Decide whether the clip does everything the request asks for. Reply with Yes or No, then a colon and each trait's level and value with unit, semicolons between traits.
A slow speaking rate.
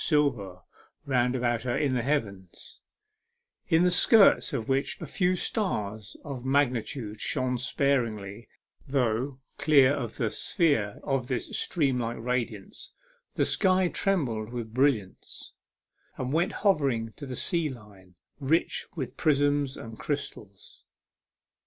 Yes: slow, 125 wpm